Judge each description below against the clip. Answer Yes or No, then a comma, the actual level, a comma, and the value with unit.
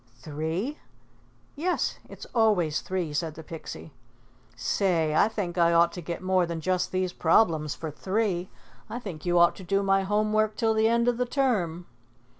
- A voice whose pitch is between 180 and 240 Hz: Yes, medium, 185 Hz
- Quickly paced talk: No, average, 180 wpm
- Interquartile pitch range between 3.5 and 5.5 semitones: Yes, average, 4.5 semitones